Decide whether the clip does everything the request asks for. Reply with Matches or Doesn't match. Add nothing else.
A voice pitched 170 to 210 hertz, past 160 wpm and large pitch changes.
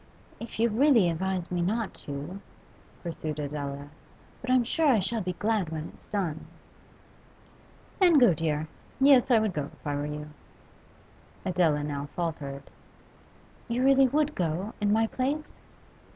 Doesn't match